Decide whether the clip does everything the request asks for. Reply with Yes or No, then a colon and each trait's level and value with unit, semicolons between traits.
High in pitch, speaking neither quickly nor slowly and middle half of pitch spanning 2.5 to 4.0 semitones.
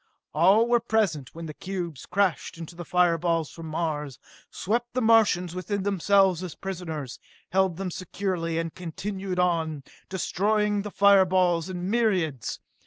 No: medium, 180 Hz; average, 150 wpm; average, 3.2 semitones